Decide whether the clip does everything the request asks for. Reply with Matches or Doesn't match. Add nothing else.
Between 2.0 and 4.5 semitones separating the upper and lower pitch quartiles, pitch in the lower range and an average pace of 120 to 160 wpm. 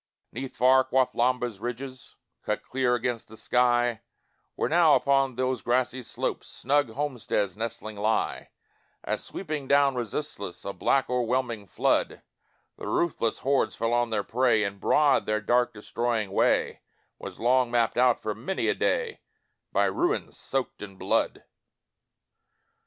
Matches